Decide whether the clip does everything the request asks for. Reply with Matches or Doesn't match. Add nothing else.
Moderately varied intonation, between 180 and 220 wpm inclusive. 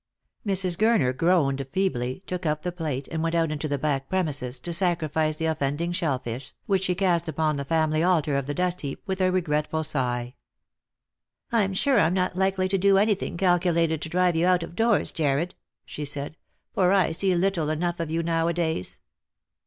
Matches